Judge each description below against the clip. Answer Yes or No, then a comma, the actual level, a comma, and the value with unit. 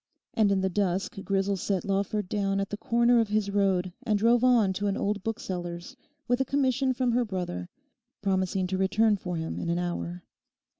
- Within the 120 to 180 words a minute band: No, average, 195 wpm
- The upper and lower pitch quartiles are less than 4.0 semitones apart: Yes, average, 3.2 semitones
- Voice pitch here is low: No, high, 200 Hz